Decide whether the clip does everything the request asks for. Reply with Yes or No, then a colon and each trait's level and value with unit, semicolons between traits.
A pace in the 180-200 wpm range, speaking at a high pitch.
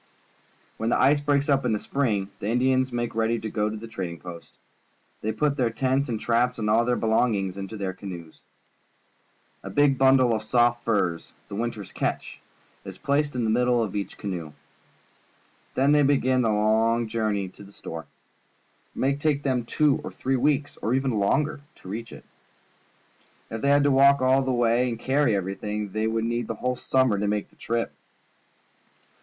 No: average, 195 wpm; low, 115 Hz